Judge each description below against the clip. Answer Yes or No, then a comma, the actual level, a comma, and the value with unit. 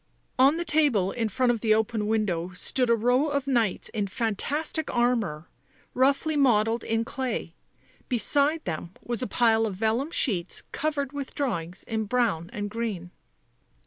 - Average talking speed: Yes, average, 155 wpm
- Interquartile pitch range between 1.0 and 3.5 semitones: No, average, 4.3 semitones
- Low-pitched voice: No, high, 230 Hz